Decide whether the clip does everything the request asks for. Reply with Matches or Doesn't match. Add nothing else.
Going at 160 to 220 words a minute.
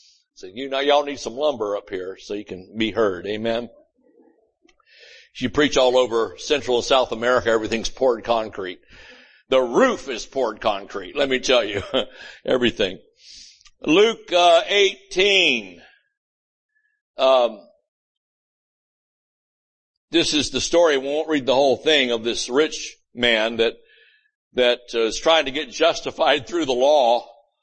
Doesn't match